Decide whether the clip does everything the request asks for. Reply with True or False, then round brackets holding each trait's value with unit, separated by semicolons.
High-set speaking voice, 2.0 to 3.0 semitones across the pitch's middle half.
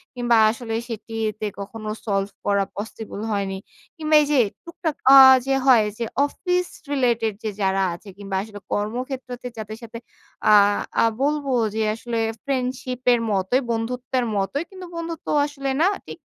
False (235 Hz; 4.2 semitones)